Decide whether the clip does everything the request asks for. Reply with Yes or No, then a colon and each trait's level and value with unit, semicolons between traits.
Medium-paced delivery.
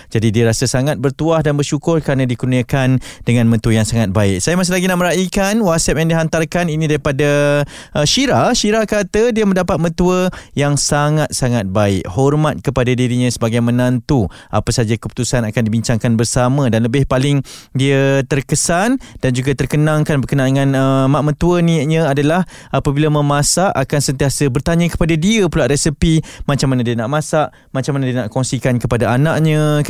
No: fast, 160 wpm